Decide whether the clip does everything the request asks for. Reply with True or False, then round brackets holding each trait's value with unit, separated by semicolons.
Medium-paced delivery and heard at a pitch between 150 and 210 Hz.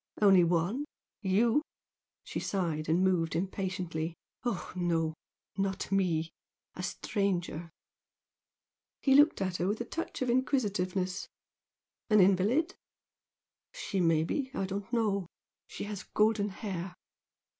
False (120 wpm; 190 Hz)